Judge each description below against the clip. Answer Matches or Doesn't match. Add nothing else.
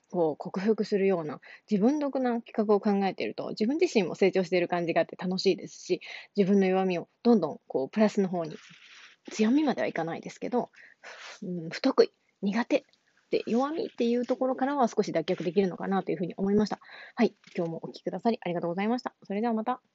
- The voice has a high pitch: Matches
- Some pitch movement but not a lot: Matches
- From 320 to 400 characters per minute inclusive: Doesn't match